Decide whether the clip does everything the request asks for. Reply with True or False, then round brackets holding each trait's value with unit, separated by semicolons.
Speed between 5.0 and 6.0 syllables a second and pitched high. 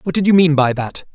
False (5.9 syllables/s; 155 Hz)